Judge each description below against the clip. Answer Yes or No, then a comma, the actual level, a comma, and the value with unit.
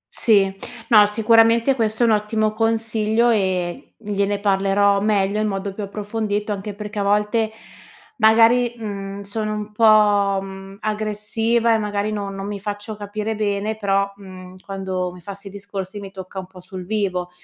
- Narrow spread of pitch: Yes, narrow, 1.7 semitones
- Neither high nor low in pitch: No, high, 205 Hz